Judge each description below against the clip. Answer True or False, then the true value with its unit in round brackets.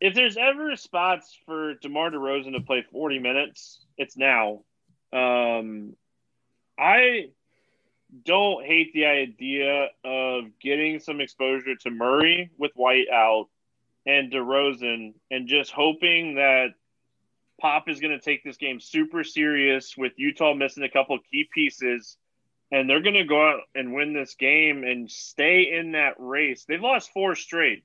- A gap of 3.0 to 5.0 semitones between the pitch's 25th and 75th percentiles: True (3.5 semitones)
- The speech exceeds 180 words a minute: False (150 wpm)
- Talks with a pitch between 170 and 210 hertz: False (140 Hz)